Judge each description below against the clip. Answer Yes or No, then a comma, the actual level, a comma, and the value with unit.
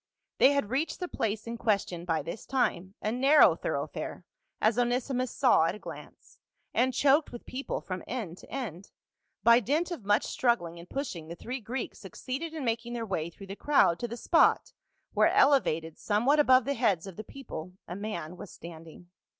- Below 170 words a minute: No, average, 190 wpm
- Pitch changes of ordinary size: No, wide, 6.4 semitones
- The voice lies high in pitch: Yes, high, 230 Hz